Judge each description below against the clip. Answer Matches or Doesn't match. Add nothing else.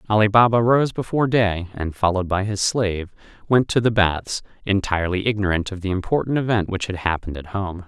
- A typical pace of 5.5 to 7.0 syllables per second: Matches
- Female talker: Doesn't match